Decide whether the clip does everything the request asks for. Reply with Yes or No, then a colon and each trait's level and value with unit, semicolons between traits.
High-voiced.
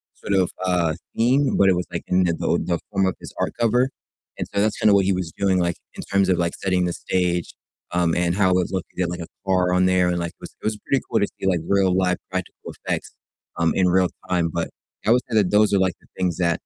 No: very low, 90 Hz